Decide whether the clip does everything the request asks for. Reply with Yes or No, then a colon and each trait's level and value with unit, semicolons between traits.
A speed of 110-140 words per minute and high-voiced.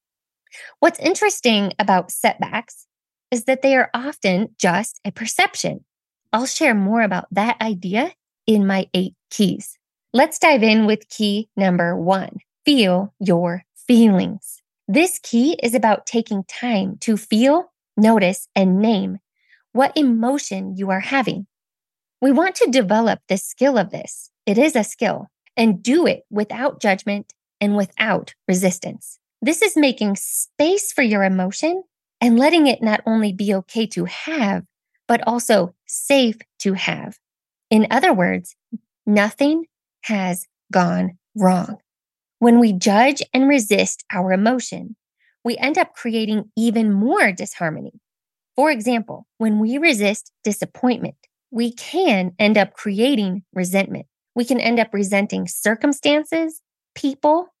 Yes: slow, 135 wpm; high, 225 Hz